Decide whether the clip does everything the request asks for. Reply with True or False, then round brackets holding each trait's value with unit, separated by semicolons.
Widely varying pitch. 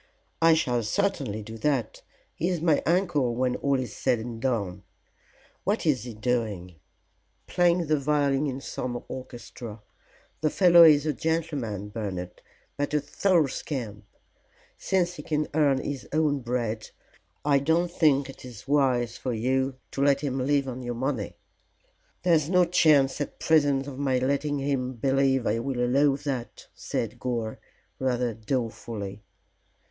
False (3.8 semitones)